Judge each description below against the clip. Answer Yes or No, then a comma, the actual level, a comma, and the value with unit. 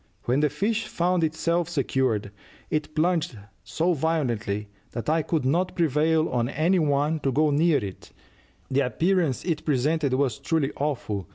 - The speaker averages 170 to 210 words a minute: No, average, 155 wpm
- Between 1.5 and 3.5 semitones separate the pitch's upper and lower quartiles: No, average, 3.9 semitones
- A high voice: No, medium, 150 Hz